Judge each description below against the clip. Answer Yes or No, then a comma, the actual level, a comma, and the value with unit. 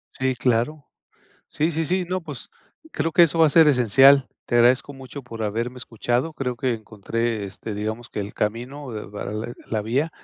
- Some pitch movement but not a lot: Yes, average, 4.3 semitones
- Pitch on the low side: Yes, low, 125 Hz